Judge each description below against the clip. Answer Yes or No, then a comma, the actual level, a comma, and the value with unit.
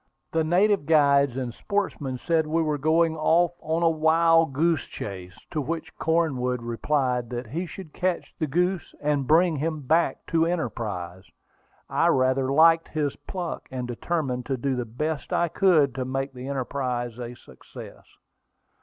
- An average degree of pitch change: Yes, average, 4.4 semitones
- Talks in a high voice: No, medium, 150 Hz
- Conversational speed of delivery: Yes, average, 160 wpm